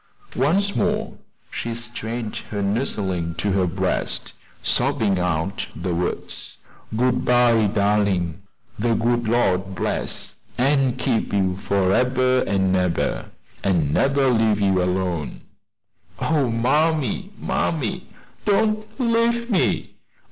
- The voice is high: No, low, 110 Hz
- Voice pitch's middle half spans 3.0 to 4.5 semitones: No, wide, 5.4 semitones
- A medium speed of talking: No, slow, 110 wpm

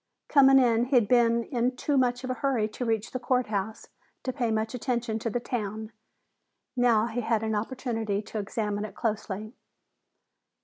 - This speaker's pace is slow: No, average, 175 wpm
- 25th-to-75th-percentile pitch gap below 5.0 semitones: Yes, narrow, 2.5 semitones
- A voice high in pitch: Yes, high, 230 Hz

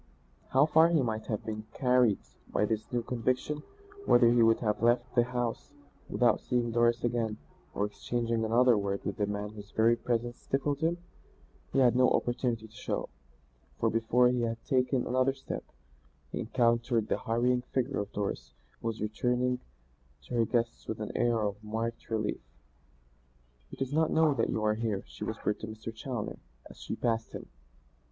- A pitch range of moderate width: No, narrow, 2.3 semitones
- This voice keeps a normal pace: Yes, average, 175 wpm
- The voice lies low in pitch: Yes, low, 115 Hz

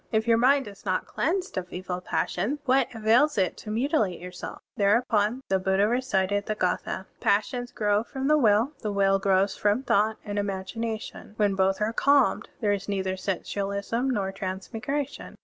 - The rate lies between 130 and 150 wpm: No, average, 170 wpm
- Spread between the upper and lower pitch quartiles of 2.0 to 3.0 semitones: No, average, 3.7 semitones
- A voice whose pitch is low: No, high, 205 Hz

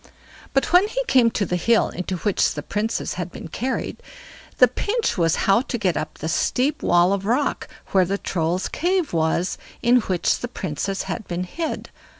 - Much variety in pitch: Yes, wide, 6.1 semitones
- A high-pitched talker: Yes, high, 200 Hz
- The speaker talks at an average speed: Yes, average, 185 wpm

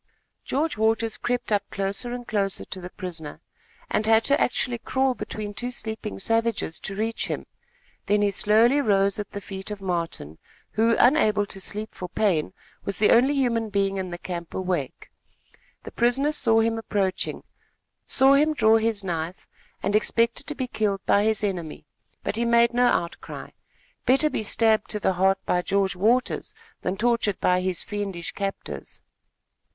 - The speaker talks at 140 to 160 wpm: No, average, 170 wpm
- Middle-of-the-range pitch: No, high, 210 Hz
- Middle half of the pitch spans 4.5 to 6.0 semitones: No, average, 3.3 semitones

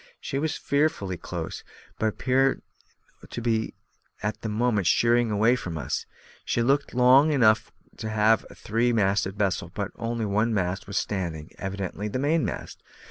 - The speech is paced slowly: No, average, 150 wpm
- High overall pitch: No, low, 110 Hz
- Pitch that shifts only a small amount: No, average, 3.7 semitones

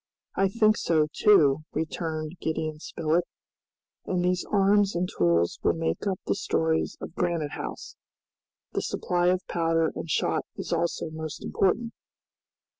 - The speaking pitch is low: No, medium, 165 Hz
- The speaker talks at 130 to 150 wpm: Yes, average, 140 wpm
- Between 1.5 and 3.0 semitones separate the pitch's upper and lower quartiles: Yes, average, 2.7 semitones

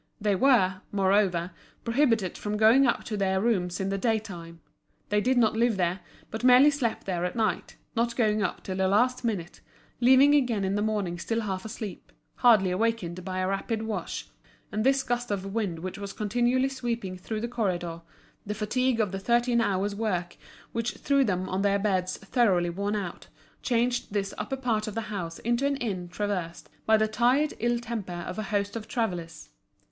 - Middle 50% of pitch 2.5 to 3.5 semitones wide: No, average, 3.9 semitones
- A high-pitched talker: Yes, high, 210 Hz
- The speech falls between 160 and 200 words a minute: Yes, average, 190 wpm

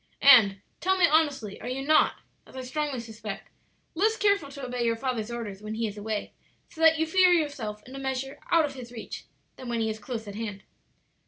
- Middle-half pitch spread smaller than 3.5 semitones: No, wide, 5.4 semitones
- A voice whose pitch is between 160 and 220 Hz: No, very high, 255 Hz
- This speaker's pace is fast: Yes, fast, 220 wpm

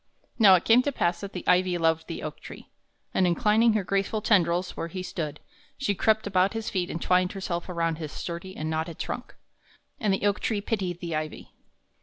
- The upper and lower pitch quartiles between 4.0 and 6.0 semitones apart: No, average, 3.2 semitones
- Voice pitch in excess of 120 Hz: Yes, medium, 185 Hz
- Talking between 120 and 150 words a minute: No, fast, 205 wpm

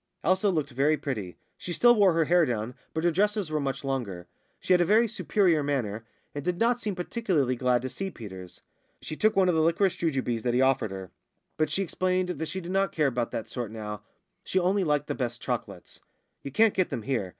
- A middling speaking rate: No, fast, 225 wpm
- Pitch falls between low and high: Yes, medium, 155 Hz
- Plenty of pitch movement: Yes, wide, 7.1 semitones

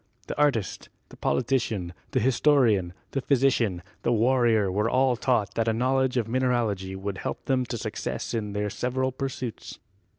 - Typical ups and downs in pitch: Yes, average, 4.0 semitones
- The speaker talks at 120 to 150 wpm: No, average, 160 wpm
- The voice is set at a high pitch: No, low, 120 Hz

